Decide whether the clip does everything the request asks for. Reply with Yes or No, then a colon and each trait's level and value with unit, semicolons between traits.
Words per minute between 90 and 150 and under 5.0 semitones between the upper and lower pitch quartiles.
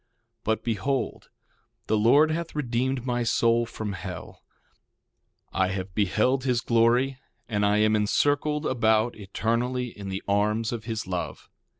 Yes: average, 140 wpm; average, 3.3 semitones